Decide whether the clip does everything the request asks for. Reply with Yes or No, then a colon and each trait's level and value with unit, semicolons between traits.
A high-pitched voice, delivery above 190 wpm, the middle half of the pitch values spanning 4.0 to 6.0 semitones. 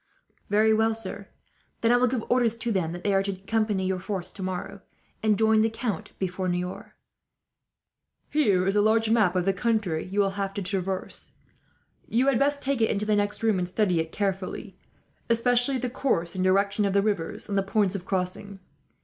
No: high, 205 Hz; average, 200 wpm; average, 3.0 semitones